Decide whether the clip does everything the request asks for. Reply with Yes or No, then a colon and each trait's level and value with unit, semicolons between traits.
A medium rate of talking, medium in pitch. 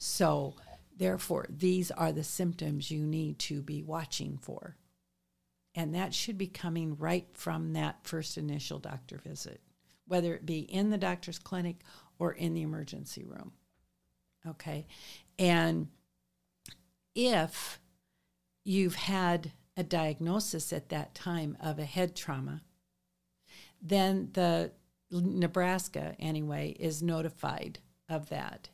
No: slow, 120 wpm; medium, 160 Hz